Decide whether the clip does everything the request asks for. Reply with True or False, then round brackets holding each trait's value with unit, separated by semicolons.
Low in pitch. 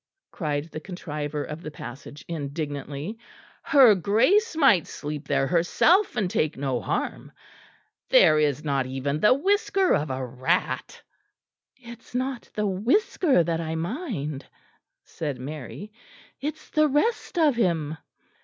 False (170 Hz)